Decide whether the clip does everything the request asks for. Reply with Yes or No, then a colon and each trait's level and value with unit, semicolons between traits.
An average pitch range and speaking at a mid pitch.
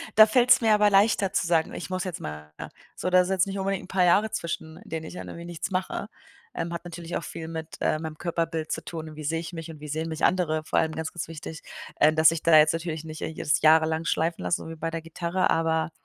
No: narrow, 2.2 semitones; medium, 165 Hz